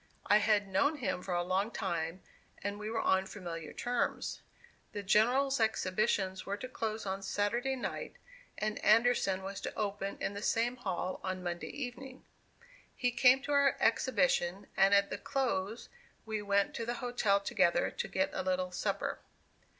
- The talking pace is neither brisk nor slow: Yes, average, 165 wpm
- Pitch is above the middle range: Yes, high, 205 Hz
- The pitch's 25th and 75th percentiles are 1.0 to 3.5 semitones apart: No, average, 4.2 semitones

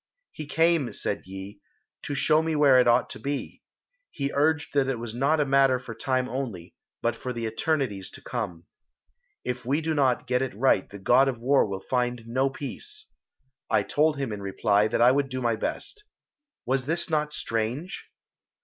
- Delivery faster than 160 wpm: Yes, average, 190 wpm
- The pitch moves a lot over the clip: No, average, 3.7 semitones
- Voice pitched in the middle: No, low, 130 Hz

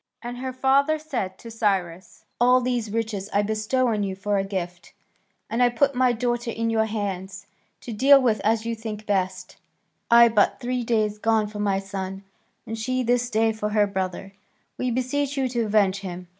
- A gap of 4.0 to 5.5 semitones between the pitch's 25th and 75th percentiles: No, average, 3.5 semitones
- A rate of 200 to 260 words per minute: Yes, fast, 205 wpm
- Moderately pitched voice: No, high, 220 Hz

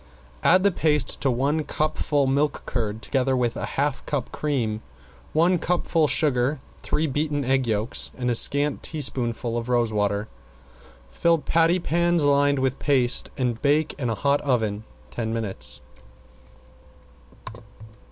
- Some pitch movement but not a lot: Yes, average, 4.2 semitones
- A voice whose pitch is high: No, low, 135 Hz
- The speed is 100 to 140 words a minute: Yes, slow, 135 wpm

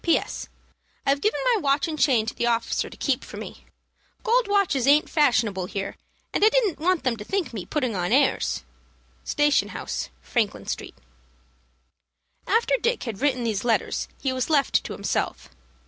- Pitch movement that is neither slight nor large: No, wide, 6.9 semitones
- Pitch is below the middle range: No, very high, 275 Hz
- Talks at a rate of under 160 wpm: No, average, 170 wpm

